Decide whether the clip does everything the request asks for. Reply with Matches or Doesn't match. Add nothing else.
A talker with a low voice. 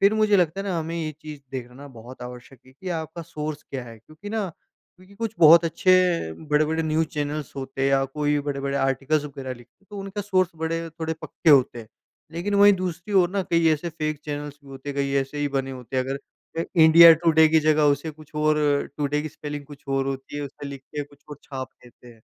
Doesn't match